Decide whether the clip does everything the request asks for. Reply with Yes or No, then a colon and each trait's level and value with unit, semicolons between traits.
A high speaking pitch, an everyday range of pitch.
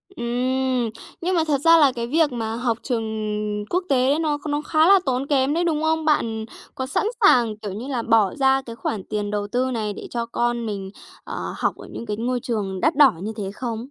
Yes: high, 245 Hz; average, 4.4 semitones